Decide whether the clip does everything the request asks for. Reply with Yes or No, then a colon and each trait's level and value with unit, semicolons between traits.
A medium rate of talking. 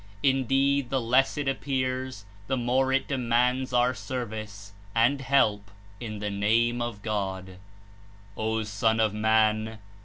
No: slow, 130 wpm